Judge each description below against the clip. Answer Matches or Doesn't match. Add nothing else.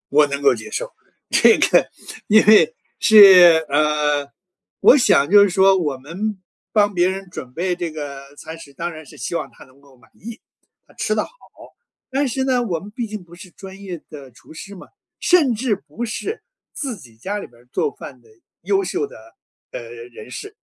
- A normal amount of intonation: Doesn't match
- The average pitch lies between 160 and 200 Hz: Matches